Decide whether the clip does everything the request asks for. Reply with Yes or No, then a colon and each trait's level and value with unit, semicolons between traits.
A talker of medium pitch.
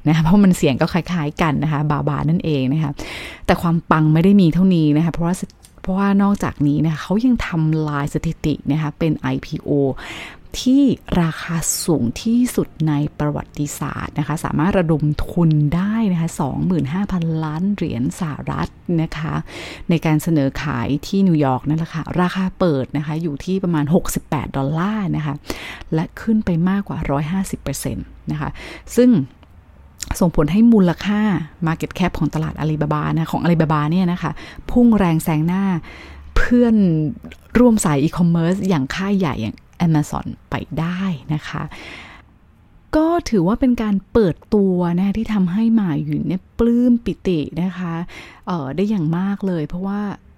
Yes: medium, 165 Hz